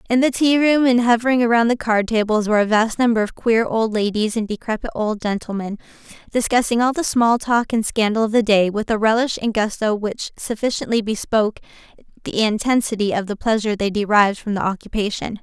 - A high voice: Yes, high, 220 Hz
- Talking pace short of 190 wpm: No, average, 195 wpm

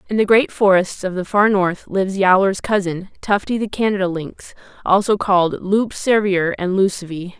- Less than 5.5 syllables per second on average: Yes, 4.9 syllables/s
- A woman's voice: Yes, female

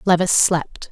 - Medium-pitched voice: Yes, medium, 175 Hz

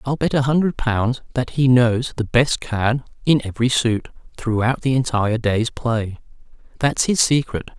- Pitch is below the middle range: Yes, low, 125 Hz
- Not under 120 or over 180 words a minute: Yes, average, 170 wpm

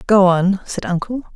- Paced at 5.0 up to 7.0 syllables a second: No, 4.6 syllables/s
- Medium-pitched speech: No, high, 195 Hz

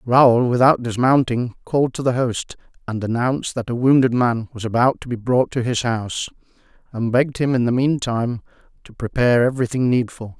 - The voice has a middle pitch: No, low, 120 Hz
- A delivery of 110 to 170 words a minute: No, average, 180 wpm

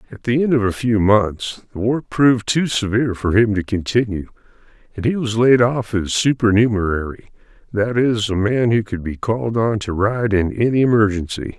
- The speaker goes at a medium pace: Yes, average, 185 wpm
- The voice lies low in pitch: Yes, low, 110 Hz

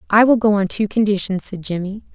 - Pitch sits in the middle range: No, high, 205 Hz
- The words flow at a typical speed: No, fast, 225 wpm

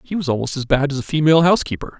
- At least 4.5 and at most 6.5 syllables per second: No, 7.9 syllables/s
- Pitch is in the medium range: Yes, medium, 145 Hz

